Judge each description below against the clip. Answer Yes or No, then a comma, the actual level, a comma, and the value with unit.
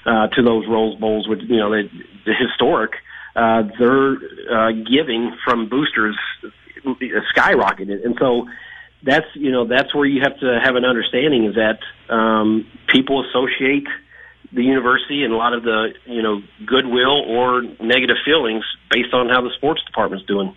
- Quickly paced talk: No, average, 165 wpm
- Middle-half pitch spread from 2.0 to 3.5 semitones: Yes, average, 2.8 semitones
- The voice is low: Yes, low, 120 Hz